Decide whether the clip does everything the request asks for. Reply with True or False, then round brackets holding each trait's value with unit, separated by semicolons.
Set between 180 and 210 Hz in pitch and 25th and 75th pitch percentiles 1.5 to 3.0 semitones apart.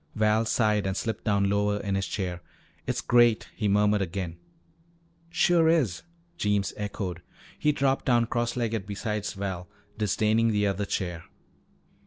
False (105 Hz; 2.6 semitones)